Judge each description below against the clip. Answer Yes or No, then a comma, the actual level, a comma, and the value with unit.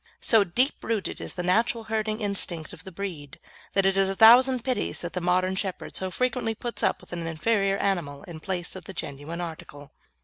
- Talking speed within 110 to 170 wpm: No, fast, 205 wpm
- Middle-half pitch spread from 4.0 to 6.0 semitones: Yes, average, 4.3 semitones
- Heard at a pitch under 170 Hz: No, high, 190 Hz